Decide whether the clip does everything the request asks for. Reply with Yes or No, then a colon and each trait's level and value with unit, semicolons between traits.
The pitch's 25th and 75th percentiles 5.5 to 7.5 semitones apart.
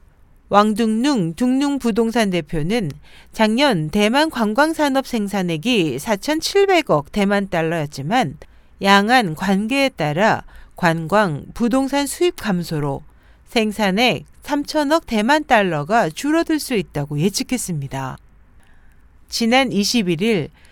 No: wide, 7.9 semitones